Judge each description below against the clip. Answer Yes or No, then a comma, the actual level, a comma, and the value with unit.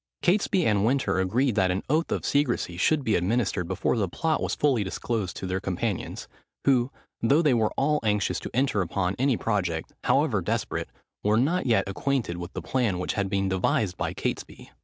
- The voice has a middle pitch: No, low, 110 Hz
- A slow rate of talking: No, average, 190 wpm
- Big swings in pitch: Yes, wide, 6.2 semitones